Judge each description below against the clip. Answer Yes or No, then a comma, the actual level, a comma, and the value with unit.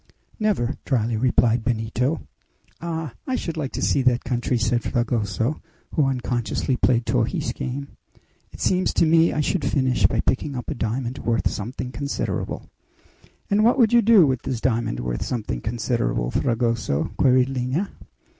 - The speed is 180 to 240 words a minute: No, average, 155 wpm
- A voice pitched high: No, low, 125 Hz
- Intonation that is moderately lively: Yes, average, 3.8 semitones